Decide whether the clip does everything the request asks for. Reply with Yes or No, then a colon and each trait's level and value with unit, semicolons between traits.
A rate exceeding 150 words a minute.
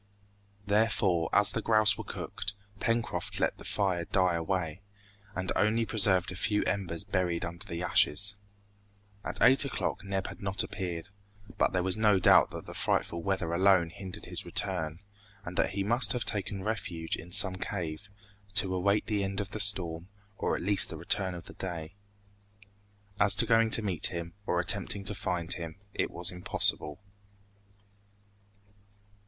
Yes: average, 165 wpm